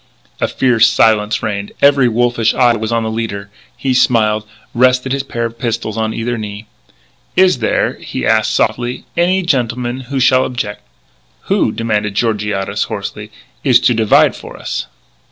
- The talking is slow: No, average, 155 wpm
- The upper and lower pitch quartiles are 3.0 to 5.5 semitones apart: No, narrow, 2.6 semitones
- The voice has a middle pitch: No, low, 115 Hz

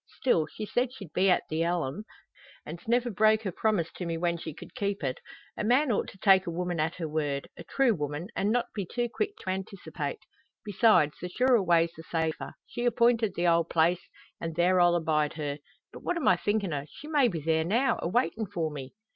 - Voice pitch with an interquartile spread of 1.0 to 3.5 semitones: No, average, 5.3 semitones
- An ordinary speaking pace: No, fast, 220 wpm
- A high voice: No, medium, 180 Hz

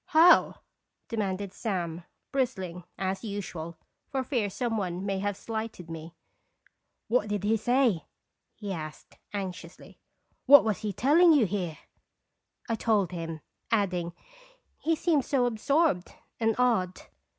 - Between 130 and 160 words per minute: Yes, average, 140 wpm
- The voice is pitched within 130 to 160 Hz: No, high, 205 Hz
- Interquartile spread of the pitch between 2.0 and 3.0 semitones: No, average, 5.2 semitones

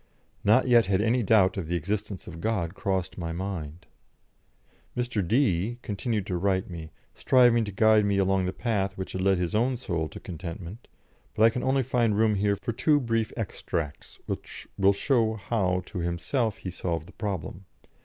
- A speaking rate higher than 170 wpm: Yes, average, 185 wpm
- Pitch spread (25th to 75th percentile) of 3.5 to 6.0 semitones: Yes, average, 3.9 semitones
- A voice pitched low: Yes, low, 100 Hz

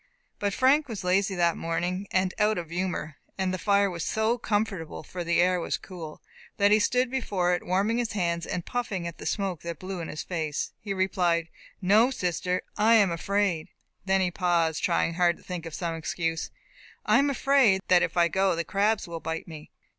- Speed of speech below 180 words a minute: No, fast, 205 wpm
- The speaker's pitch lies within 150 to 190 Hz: Yes, medium, 185 Hz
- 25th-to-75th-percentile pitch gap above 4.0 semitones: No, average, 3.2 semitones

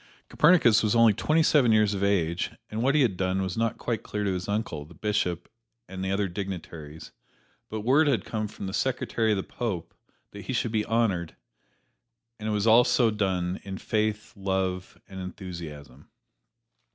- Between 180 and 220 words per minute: Yes, average, 185 wpm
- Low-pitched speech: Yes, low, 100 Hz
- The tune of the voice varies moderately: Yes, average, 3.5 semitones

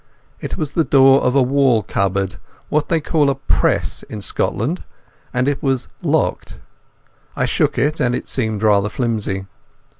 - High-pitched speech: No, low, 125 Hz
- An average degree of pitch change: Yes, average, 5.0 semitones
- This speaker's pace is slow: No, average, 150 wpm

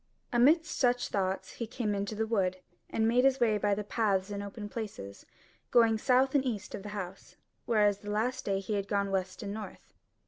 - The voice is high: Yes, high, 210 Hz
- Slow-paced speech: No, fast, 205 wpm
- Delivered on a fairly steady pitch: No, average, 3.0 semitones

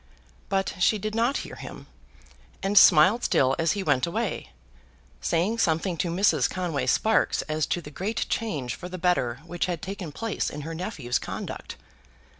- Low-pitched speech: No, medium, 175 Hz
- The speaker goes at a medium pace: Yes, average, 170 wpm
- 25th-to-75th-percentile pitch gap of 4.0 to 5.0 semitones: Yes, average, 4.5 semitones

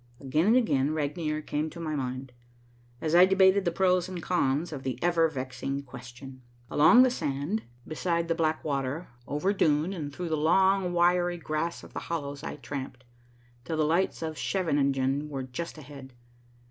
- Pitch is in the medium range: Yes, medium, 155 Hz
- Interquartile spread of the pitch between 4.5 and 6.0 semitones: No, average, 4.0 semitones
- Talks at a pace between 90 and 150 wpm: No, average, 170 wpm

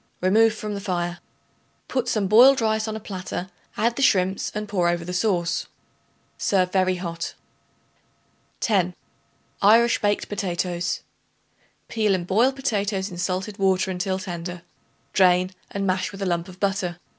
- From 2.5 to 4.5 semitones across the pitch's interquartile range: Yes, average, 2.8 semitones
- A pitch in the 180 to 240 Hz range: Yes, high, 190 Hz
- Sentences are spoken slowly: No, average, 150 wpm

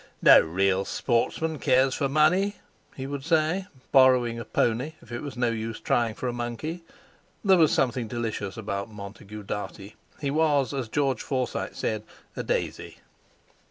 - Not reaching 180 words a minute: Yes, average, 160 wpm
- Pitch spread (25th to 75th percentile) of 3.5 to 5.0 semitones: Yes, average, 4.6 semitones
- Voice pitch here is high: No, low, 125 Hz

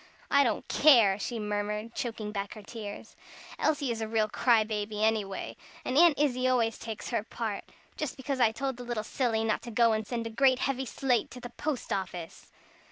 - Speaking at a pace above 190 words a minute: Yes, average, 200 wpm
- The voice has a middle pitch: No, high, 230 Hz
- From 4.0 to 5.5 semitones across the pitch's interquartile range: No, average, 3.0 semitones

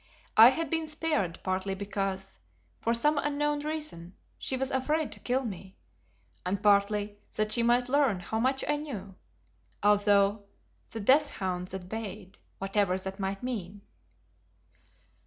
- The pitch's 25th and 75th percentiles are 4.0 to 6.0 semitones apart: Yes, wide, 5.5 semitones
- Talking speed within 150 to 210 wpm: No, average, 140 wpm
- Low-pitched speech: No, high, 210 Hz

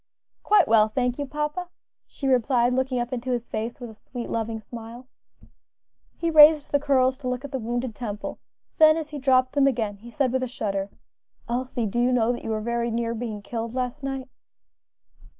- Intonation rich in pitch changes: No, average, 2.7 semitones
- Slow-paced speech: No, average, 200 wpm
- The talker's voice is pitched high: Yes, very high, 250 Hz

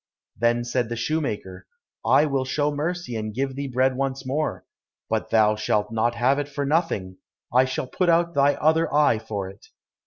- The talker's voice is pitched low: Yes, low, 130 Hz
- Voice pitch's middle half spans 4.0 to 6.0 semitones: Yes, average, 4.5 semitones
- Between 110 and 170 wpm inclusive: No, average, 185 wpm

